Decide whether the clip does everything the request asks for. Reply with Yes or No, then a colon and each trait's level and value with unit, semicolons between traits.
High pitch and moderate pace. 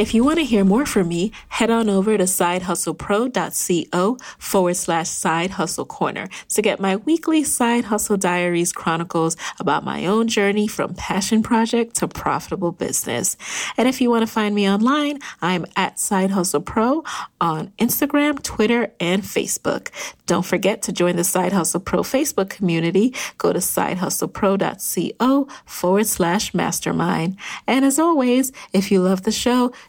Yes: high, 205 Hz; average, 150 wpm